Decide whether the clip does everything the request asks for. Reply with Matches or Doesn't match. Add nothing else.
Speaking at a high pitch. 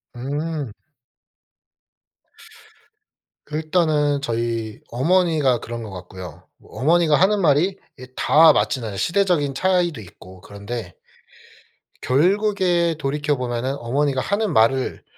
Doesn't match